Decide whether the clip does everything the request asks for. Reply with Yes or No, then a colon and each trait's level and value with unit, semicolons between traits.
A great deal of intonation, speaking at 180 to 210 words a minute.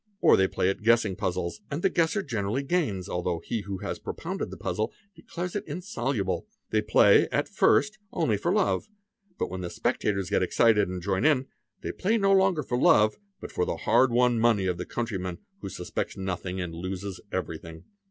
Yes: wide, 7.0 semitones; average, 190 wpm